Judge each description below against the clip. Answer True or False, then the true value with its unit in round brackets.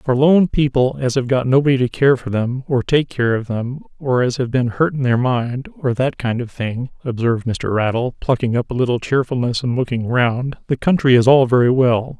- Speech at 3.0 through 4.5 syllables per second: False (5.1 syllables/s)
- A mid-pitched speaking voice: False (125 Hz)